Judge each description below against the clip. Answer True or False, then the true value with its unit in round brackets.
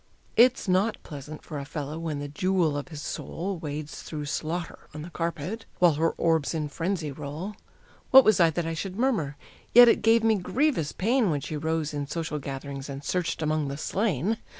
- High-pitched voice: False (160 Hz)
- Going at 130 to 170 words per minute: False (195 wpm)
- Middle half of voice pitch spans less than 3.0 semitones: False (4.4 semitones)